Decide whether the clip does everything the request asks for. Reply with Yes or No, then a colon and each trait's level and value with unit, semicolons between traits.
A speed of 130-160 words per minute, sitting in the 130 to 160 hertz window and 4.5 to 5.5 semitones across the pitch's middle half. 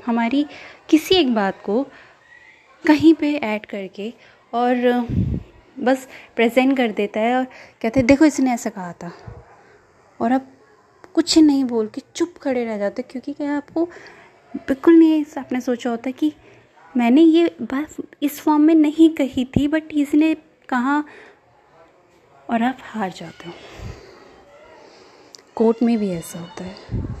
No: average, 145 wpm; very high, 265 Hz; average, 5.2 semitones